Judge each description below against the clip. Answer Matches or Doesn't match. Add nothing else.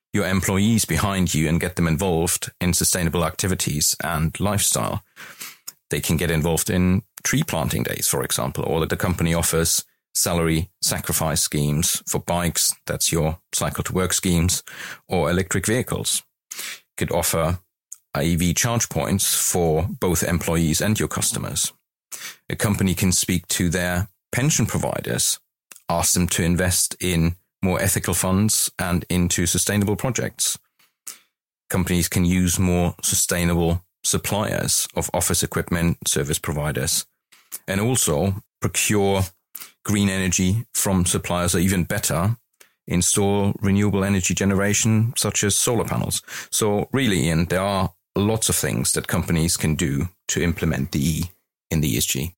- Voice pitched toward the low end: Matches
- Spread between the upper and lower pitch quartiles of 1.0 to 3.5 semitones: Matches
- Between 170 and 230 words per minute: Doesn't match